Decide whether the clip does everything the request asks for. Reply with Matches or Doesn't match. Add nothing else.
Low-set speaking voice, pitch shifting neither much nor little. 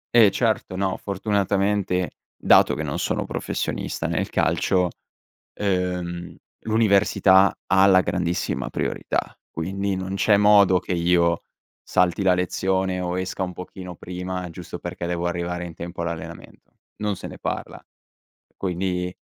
Doesn't match